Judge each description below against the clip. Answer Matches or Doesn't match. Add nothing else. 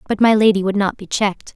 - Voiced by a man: Doesn't match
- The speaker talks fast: Matches